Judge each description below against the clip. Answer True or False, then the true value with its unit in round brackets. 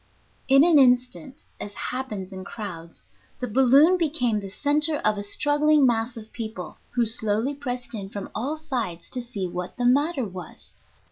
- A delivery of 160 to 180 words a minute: True (165 wpm)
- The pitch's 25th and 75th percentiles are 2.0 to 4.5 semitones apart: False (5.3 semitones)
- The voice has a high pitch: True (245 Hz)